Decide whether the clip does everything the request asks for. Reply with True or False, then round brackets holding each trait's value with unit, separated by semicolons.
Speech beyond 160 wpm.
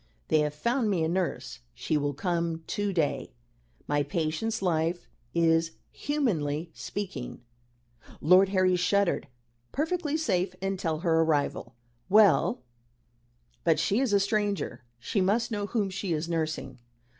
False (135 wpm)